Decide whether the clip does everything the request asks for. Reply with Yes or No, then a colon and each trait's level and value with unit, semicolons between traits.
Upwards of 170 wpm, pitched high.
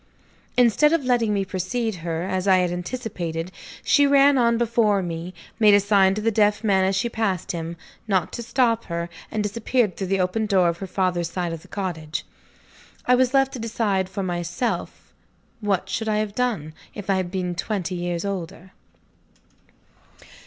Yes: average, 180 wpm; high, 195 Hz